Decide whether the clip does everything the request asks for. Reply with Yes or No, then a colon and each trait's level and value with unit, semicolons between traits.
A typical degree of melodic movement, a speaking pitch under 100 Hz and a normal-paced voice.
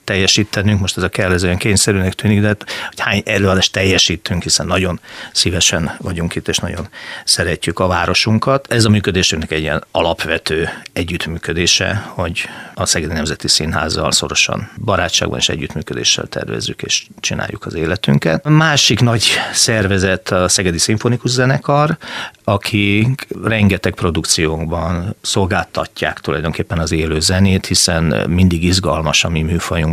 Yes: average, 4.4 semitones; very low, 90 Hz; average, 130 wpm